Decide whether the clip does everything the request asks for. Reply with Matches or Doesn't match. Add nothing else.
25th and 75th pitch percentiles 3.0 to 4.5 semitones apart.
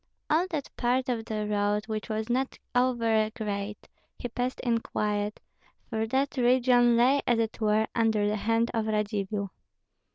Doesn't match